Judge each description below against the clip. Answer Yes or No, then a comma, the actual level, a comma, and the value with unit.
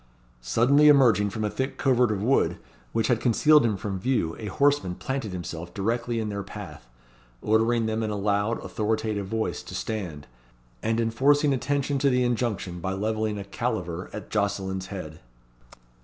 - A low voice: Yes, low, 110 Hz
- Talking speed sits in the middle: Yes, average, 165 wpm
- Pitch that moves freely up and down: No, average, 3.7 semitones